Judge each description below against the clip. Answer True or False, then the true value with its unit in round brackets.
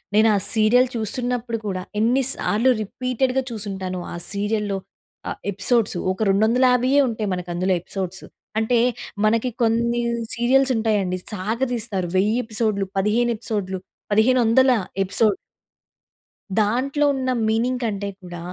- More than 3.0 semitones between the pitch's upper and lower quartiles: True (3.5 semitones)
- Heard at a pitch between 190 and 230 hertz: True (220 Hz)